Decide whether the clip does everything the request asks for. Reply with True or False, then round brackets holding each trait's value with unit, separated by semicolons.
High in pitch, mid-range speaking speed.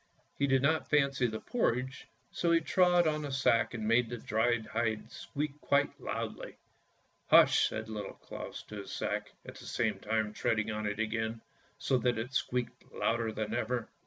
False (120 Hz; 185 wpm)